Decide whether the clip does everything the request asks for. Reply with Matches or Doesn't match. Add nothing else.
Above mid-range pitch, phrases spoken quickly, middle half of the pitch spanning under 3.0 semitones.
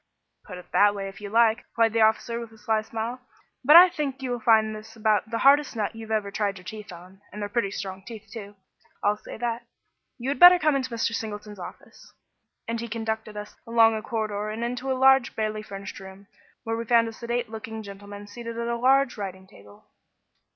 Matches